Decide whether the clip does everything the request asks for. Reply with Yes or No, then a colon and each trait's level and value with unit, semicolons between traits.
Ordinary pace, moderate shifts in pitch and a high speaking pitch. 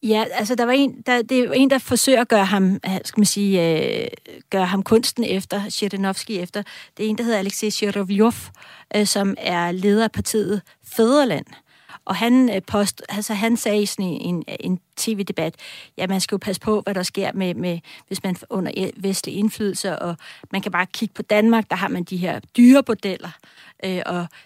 Yes: average, 200 wpm; average, 3.0 semitones; high, 205 Hz